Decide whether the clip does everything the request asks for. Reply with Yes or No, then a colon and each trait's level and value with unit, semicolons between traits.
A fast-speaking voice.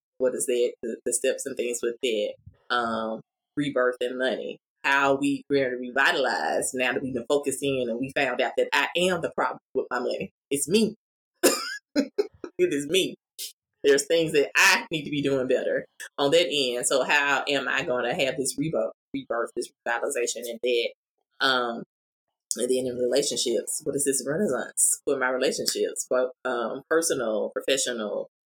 No: average, 175 wpm